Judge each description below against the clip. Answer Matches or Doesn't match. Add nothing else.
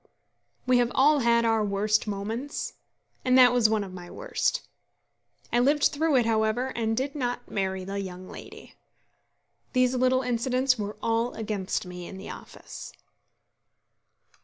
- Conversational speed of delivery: Matches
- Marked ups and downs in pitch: Doesn't match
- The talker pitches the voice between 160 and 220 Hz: Doesn't match